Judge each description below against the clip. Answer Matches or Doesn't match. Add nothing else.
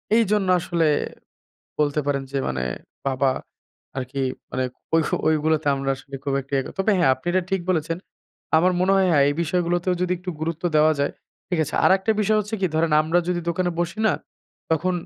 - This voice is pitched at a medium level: Matches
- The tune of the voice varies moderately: Matches